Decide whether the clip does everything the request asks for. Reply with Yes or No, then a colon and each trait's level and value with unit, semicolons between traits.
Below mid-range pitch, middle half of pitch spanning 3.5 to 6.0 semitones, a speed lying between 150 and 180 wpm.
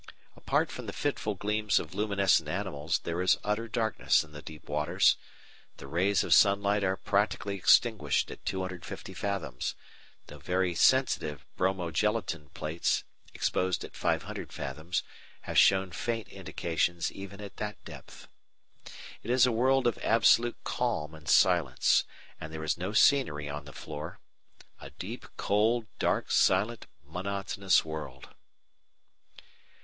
No: very low, 95 Hz; average, 5.0 semitones; slow, 135 wpm